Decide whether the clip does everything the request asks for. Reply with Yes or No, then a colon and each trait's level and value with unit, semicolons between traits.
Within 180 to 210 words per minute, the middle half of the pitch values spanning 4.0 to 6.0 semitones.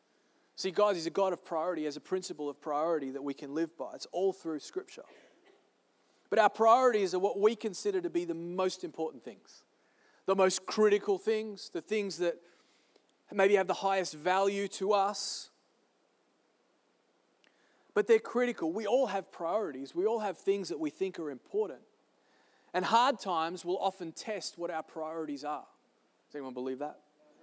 No: average, 170 wpm; average, 5.1 semitones